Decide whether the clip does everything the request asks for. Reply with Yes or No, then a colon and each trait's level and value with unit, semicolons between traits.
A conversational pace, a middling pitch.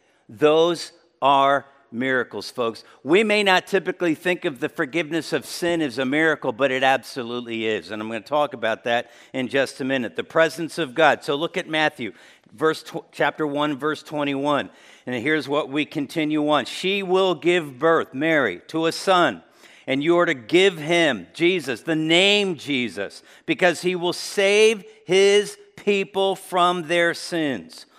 Yes: average, 165 wpm; medium, 160 Hz